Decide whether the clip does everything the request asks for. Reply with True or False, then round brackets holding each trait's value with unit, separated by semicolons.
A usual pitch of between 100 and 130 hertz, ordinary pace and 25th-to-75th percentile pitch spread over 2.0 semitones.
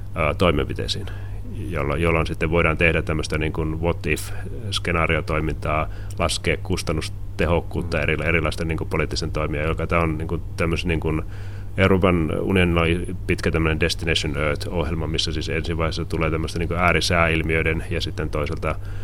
False (85 Hz; 135 wpm; 2.5 semitones)